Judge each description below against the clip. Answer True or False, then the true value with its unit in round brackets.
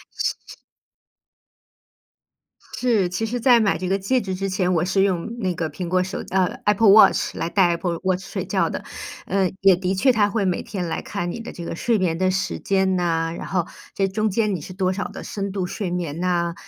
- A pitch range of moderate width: False (2.1 semitones)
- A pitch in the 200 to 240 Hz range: False (190 Hz)